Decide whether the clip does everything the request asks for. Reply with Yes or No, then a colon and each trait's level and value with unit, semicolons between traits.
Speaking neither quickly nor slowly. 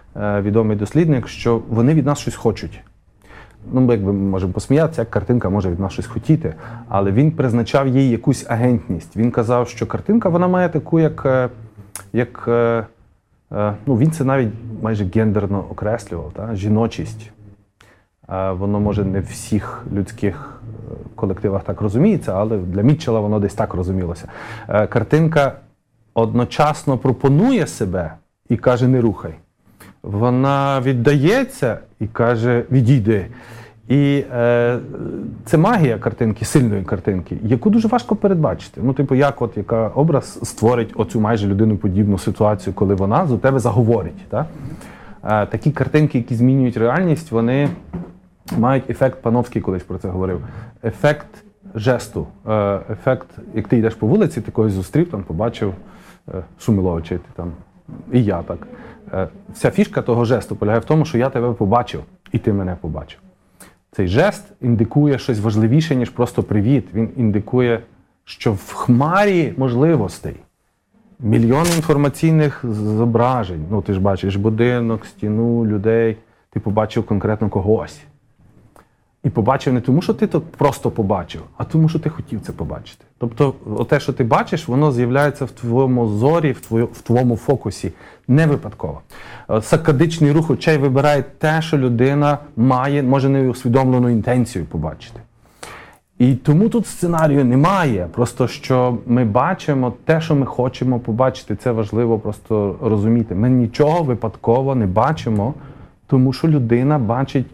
Yes: average, 140 wpm